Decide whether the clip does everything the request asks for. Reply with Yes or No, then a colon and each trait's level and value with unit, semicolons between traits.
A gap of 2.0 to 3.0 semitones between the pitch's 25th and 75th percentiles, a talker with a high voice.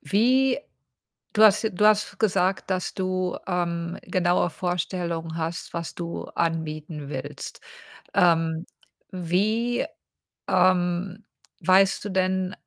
No: narrow, 2.5 semitones; medium, 180 Hz